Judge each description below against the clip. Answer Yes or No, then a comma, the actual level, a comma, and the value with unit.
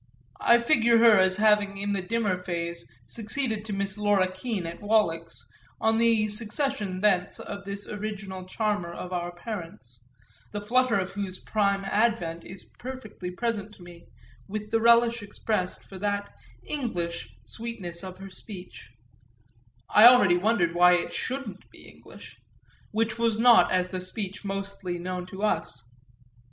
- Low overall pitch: No, high, 200 Hz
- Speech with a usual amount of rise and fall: Yes, average, 3.4 semitones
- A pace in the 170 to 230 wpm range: No, average, 150 wpm